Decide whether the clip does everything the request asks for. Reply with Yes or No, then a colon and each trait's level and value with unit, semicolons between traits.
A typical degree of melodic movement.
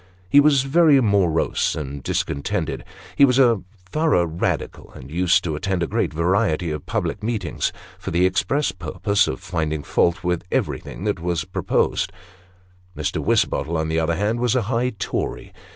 No: wide, 6.3 semitones